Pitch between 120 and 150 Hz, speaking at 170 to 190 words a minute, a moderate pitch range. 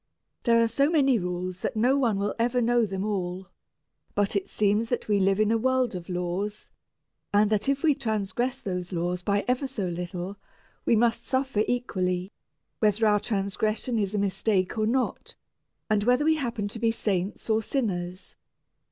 No: high, 215 Hz; average, 180 wpm; average, 4.0 semitones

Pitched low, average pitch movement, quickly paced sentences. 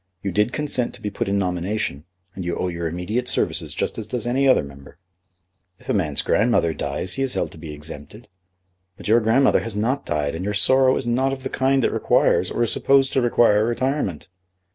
No: low, 110 Hz; wide, 6.6 semitones; fast, 215 wpm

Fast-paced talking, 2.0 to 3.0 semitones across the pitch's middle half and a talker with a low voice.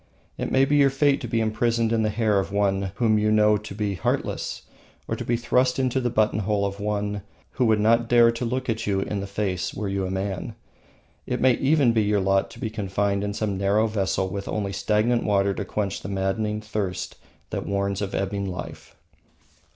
Yes: fast, 210 wpm; average, 2.7 semitones; low, 105 Hz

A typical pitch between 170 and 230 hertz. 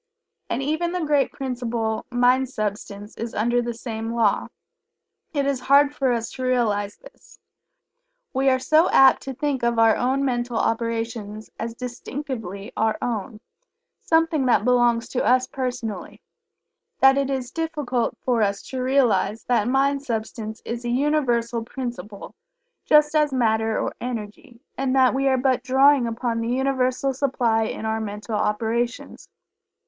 No: high, 245 Hz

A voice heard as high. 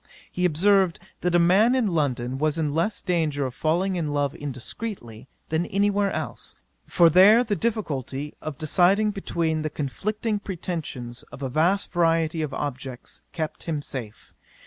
No: medium, 165 Hz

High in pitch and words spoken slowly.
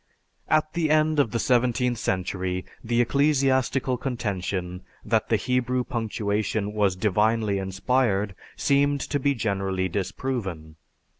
No: low, 115 Hz; slow, 120 wpm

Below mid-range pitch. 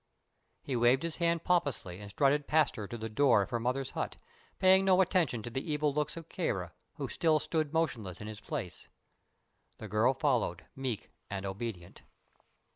Yes: low, 130 Hz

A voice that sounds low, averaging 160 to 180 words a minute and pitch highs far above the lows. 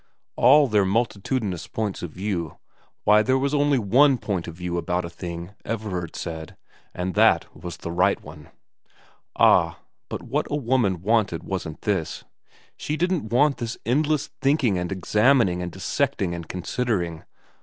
Yes: low, 100 Hz; average, 165 wpm; wide, 6.2 semitones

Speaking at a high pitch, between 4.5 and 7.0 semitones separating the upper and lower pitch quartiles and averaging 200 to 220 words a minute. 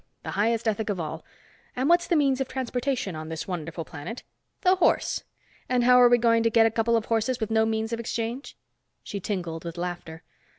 Yes: high, 225 Hz; wide, 5.4 semitones; fast, 205 wpm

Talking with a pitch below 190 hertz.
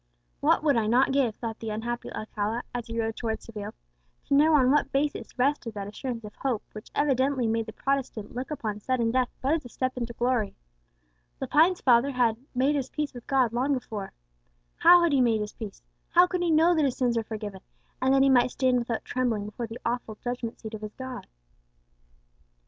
No: high, 245 Hz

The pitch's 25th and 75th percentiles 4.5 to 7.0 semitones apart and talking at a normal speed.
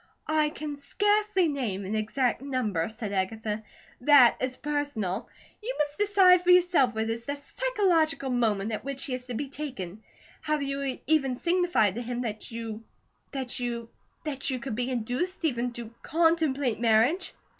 Yes: average, 5.2 semitones; average, 165 wpm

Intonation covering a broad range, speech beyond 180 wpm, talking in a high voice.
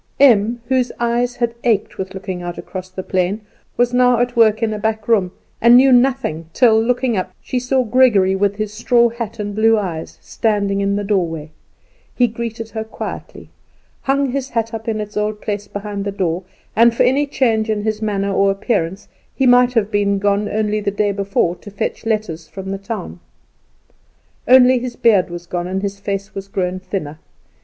No: average, 3.2 semitones; average, 195 wpm; high, 210 Hz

